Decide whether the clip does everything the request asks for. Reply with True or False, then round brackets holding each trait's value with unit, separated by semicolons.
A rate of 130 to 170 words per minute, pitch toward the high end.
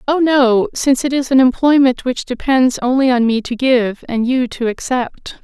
False (200 wpm; 255 Hz)